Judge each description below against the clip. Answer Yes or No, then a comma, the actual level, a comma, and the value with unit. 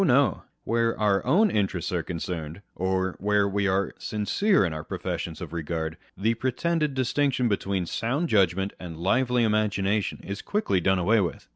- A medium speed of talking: Yes, average, 160 wpm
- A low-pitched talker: Yes, low, 100 Hz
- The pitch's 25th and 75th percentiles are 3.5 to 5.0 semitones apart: Yes, average, 3.9 semitones